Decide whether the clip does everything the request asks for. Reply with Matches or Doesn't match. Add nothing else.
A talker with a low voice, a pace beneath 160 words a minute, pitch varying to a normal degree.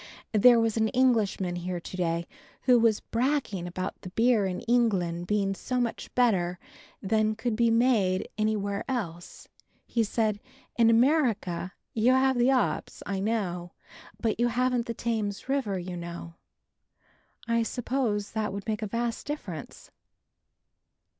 Doesn't match